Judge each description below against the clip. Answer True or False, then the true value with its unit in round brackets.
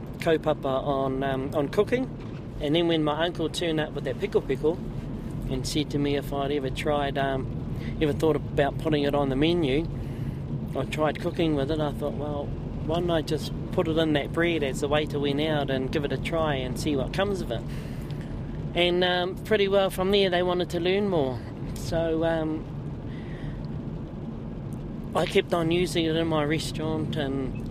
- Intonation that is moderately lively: True (3.4 semitones)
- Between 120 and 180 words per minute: False (195 wpm)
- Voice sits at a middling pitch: True (150 Hz)